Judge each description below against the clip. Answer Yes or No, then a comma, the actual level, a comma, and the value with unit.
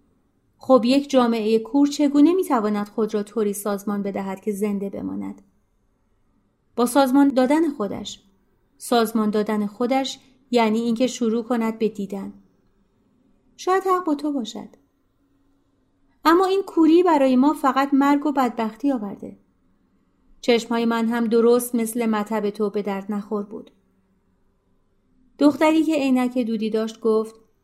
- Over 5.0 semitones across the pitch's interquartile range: No, average, 4.6 semitones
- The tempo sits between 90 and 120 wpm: No, average, 130 wpm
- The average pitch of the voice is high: Yes, high, 225 Hz